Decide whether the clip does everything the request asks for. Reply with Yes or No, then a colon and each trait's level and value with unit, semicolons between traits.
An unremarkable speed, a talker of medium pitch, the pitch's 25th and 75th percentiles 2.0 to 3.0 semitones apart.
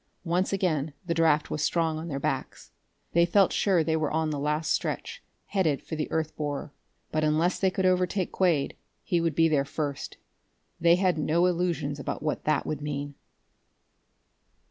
Yes: average, 175 wpm; medium, 160 Hz; average, 2.7 semitones